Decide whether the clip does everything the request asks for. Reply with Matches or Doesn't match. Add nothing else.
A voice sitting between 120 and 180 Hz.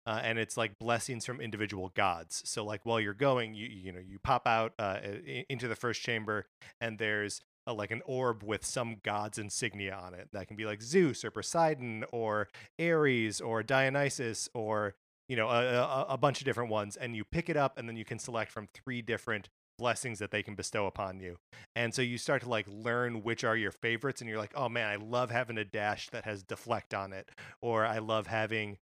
Doesn't match